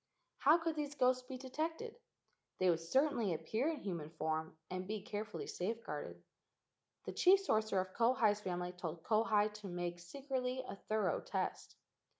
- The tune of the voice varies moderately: No, wide, 6.5 semitones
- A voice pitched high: Yes, high, 215 Hz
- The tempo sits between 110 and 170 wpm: Yes, average, 155 wpm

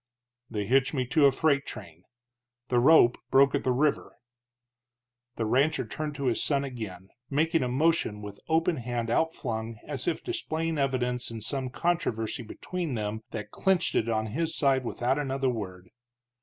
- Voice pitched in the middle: No, low, 130 Hz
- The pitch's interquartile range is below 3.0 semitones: No, average, 4.9 semitones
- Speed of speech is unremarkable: Yes, average, 165 wpm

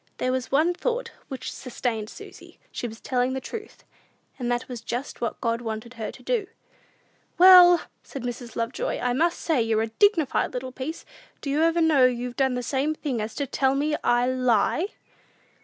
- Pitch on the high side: Yes, very high, 255 Hz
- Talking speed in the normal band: Yes, average, 185 wpm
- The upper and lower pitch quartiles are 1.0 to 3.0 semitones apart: No, average, 4.4 semitones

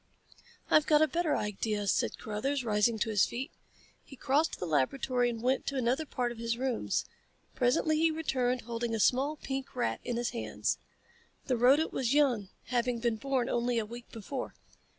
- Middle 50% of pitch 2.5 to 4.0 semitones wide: Yes, average, 2.8 semitones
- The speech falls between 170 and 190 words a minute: Yes, average, 180 wpm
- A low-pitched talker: No, high, 245 Hz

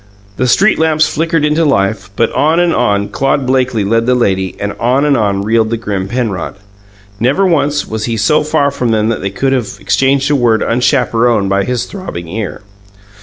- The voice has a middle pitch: No, low, 120 Hz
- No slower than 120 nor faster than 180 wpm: No, average, 195 wpm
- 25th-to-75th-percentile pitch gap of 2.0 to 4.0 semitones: No, average, 5.1 semitones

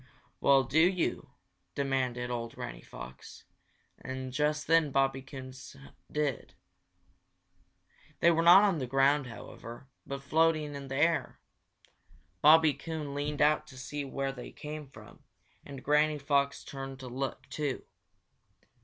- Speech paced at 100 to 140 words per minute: Yes, slow, 135 wpm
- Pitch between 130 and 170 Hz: Yes, medium, 140 Hz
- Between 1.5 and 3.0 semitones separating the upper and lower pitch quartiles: Yes, narrow, 2.4 semitones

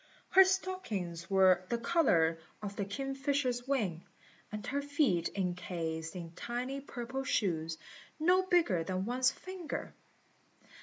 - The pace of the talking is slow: Yes, slow, 120 wpm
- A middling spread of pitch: No, wide, 8.0 semitones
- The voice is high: Yes, high, 235 Hz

